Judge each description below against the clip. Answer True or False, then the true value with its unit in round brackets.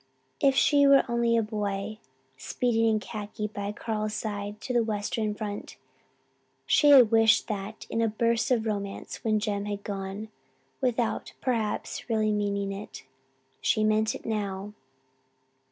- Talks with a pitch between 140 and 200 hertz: False (215 Hz)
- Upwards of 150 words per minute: False (145 wpm)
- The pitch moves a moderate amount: False (1.8 semitones)